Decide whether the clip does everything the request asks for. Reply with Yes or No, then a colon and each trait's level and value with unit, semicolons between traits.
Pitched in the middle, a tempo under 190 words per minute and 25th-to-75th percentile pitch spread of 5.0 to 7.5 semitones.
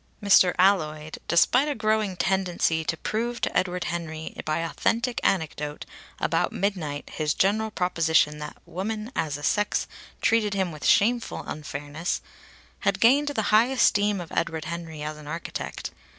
Yes: medium, 180 Hz; average, 150 wpm; average, 5.3 semitones